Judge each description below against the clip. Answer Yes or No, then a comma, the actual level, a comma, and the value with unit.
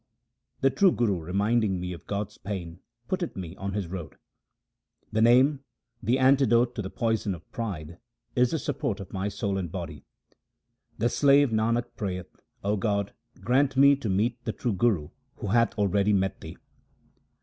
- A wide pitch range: No, average, 4.1 semitones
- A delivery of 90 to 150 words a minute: No, average, 165 wpm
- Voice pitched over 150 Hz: No, low, 105 Hz